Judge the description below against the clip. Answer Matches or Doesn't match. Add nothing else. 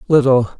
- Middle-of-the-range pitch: Matches